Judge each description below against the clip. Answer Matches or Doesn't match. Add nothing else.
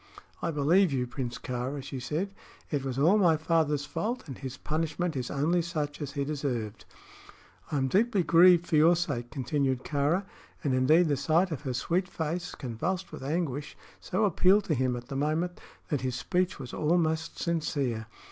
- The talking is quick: Doesn't match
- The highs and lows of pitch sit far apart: Doesn't match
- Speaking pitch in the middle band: Matches